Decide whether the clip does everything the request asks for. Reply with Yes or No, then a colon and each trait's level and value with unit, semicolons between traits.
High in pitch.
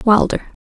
Yes: high, 210 Hz